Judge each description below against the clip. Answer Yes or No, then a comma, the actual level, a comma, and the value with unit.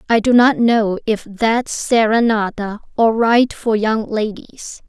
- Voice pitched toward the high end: Yes, high, 225 Hz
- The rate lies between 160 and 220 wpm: No, average, 150 wpm